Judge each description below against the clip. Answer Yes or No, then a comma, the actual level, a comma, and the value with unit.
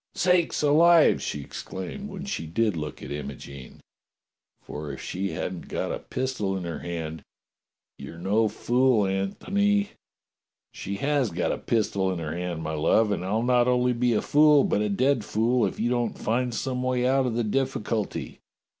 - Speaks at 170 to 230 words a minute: Yes, average, 180 wpm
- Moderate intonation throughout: No, wide, 6.1 semitones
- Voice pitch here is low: Yes, low, 110 Hz